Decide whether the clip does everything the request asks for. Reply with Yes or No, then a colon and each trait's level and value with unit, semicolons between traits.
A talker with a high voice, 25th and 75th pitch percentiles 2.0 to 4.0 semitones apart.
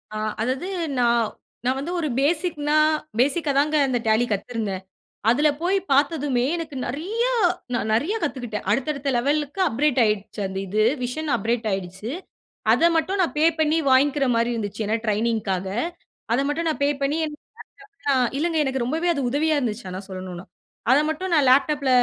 No: very high, 270 Hz; average, 5.0 semitones